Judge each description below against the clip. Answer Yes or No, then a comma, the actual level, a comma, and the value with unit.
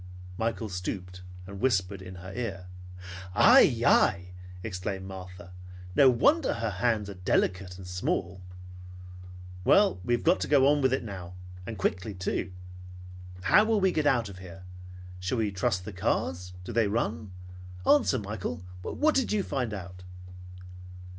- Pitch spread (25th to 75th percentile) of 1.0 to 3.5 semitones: No, average, 4.8 semitones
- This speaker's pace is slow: No, average, 155 wpm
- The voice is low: Yes, low, 100 Hz